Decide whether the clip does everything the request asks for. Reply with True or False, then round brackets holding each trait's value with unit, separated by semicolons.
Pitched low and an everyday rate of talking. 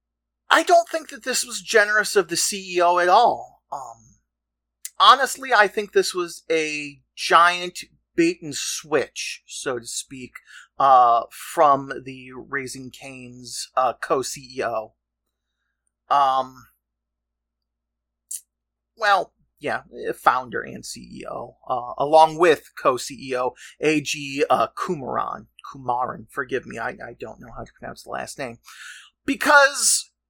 False (130 Hz; 125 wpm)